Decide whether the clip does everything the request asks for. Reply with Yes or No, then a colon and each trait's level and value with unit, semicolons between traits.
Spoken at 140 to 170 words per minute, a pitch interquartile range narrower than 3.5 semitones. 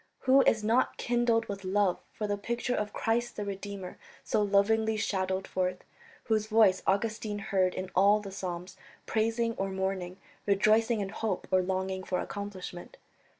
Yes: average, 155 wpm; narrow, 2.6 semitones